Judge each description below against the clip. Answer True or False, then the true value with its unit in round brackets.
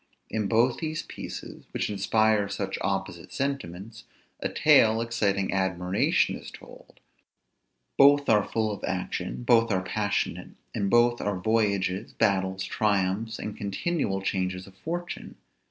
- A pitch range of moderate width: True (3.1 semitones)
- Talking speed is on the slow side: True (130 wpm)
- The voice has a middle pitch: False (105 Hz)